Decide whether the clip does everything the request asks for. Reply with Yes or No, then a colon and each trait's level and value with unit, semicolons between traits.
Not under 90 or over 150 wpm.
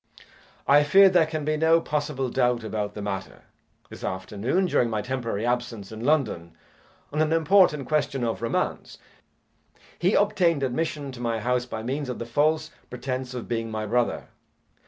No: average, 165 wpm